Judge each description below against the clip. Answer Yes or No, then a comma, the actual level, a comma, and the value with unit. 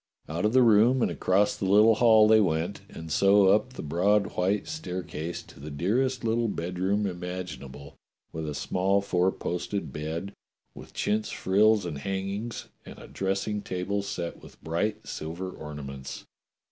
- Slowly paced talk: No, average, 160 wpm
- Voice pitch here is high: No, very low, 95 Hz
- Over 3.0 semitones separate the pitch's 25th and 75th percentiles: Yes, average, 3.7 semitones